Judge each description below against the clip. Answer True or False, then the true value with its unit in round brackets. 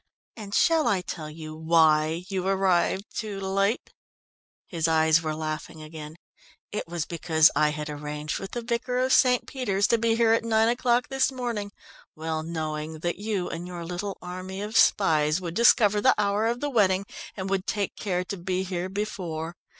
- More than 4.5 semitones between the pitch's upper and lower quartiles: True (5.0 semitones)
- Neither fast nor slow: True (180 wpm)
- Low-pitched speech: False (185 Hz)